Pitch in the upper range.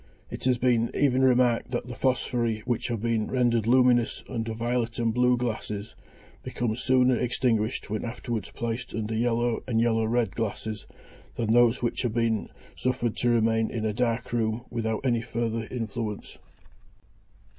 No: low, 115 Hz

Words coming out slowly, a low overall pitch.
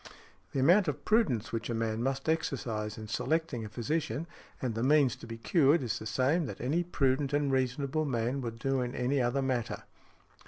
No: average, 195 wpm; low, 130 Hz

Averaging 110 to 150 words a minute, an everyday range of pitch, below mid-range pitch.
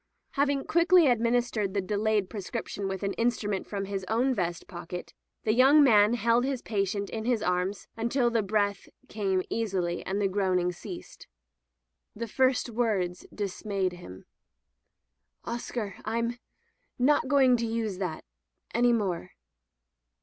No: average, 145 wpm; average, 3.8 semitones; high, 210 Hz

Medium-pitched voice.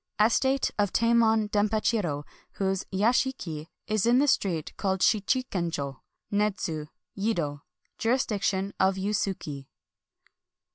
No: high, 205 Hz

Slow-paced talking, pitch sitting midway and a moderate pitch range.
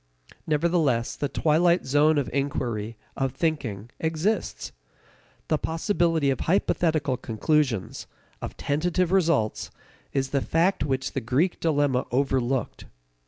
Yes: slow, 115 wpm; medium, 145 Hz; average, 4.0 semitones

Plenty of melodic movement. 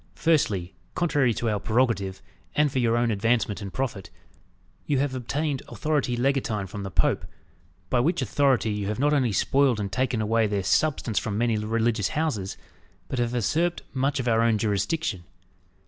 No: average, 4.6 semitones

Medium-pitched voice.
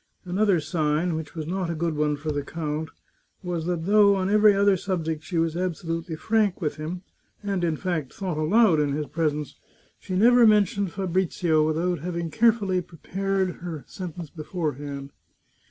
Yes: medium, 170 Hz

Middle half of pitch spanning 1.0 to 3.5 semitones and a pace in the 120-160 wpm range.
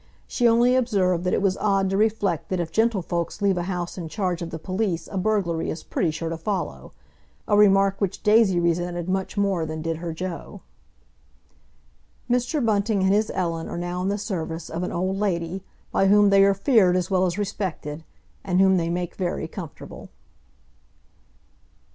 No: average, 2.9 semitones; average, 180 wpm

